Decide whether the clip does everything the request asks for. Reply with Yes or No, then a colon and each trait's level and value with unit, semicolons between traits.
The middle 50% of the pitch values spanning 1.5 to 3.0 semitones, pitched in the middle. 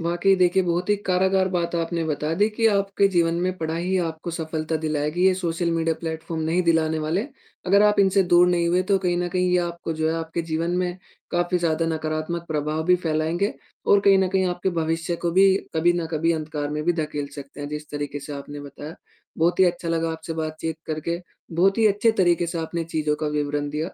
Yes: narrow, 2.4 semitones; medium, 170 Hz